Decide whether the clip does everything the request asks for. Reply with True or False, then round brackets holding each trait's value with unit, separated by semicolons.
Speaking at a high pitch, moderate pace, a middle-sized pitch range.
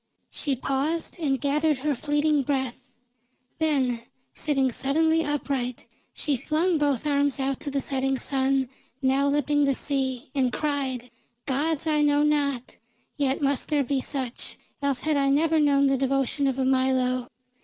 False (275 Hz; 155 wpm; 1.9 semitones)